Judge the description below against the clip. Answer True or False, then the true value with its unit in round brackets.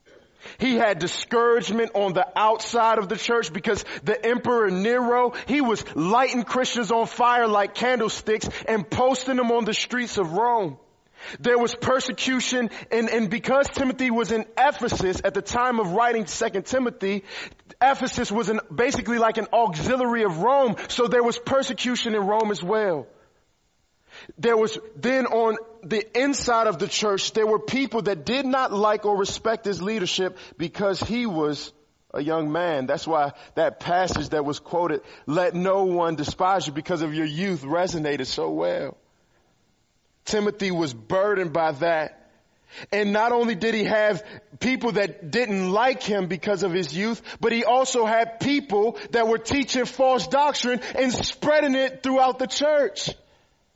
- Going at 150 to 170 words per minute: True (160 wpm)